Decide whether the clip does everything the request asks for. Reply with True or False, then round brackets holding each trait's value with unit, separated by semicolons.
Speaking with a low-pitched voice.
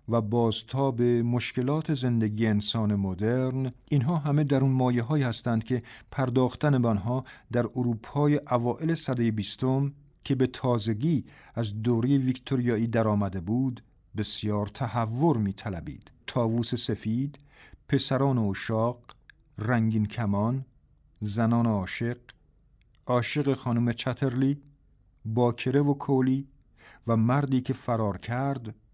True (120 Hz)